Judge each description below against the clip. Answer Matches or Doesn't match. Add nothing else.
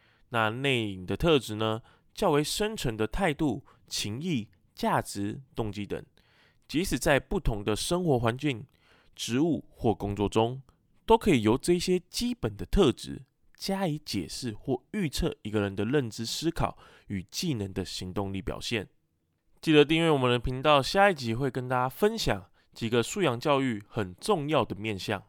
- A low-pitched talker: Matches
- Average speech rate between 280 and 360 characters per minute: Doesn't match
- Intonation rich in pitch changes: Matches